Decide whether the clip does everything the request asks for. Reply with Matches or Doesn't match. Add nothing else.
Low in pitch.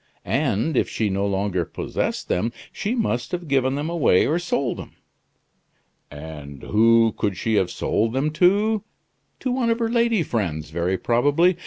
Matches